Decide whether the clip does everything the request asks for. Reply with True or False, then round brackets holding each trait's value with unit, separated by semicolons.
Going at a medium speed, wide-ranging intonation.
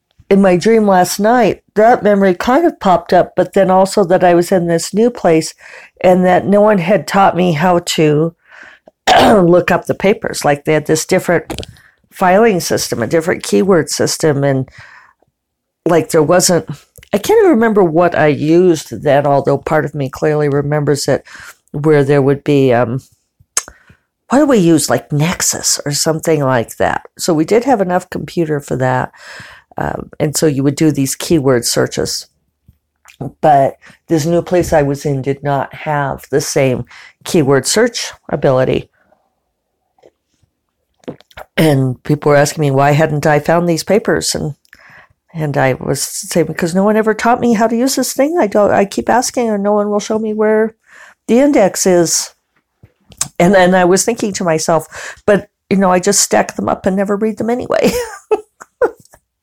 True (175 wpm; 5.7 semitones)